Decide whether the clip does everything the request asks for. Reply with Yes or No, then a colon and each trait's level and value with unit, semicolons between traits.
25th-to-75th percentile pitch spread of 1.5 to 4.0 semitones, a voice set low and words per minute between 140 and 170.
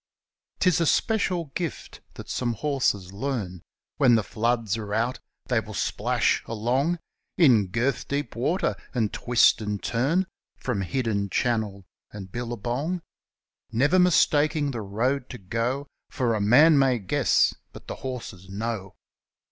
No: average, 4.9 semitones; low, 120 Hz; average, 145 wpm